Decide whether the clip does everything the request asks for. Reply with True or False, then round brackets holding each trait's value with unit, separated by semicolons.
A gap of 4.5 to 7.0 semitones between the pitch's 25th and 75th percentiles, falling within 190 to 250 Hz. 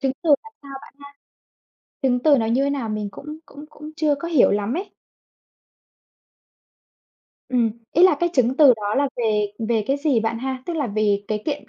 False (5.0 semitones; 260 Hz)